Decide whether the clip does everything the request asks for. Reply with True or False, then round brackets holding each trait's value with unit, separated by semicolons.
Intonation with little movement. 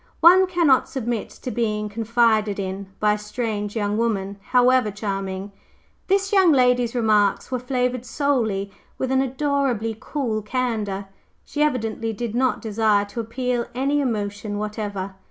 False (3.6 semitones)